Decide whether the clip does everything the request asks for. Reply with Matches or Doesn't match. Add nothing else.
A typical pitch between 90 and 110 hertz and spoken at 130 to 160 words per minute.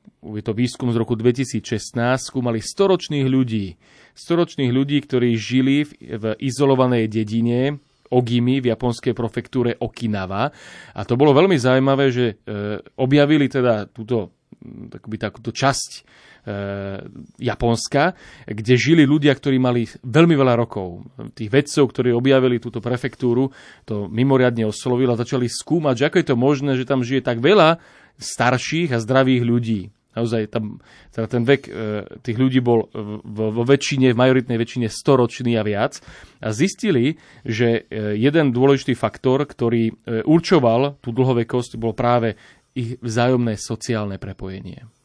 Doesn't match